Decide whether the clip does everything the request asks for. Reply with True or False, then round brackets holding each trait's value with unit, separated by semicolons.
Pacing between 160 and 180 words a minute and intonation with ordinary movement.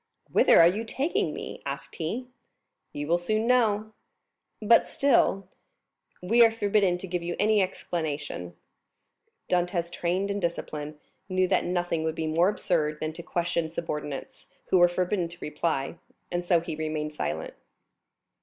False (150 wpm; 4.0 semitones)